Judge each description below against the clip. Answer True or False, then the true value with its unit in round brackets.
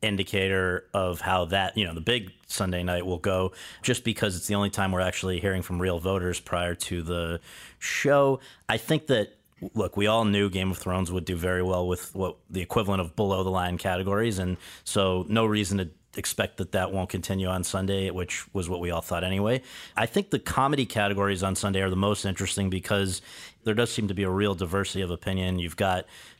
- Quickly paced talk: True (215 wpm)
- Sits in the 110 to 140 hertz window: False (95 Hz)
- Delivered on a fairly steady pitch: True (2.2 semitones)